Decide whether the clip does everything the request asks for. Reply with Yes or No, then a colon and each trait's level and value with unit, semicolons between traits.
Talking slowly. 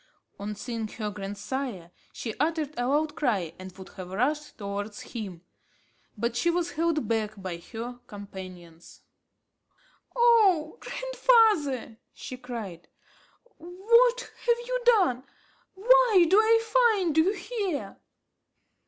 Yes: slow, 120 wpm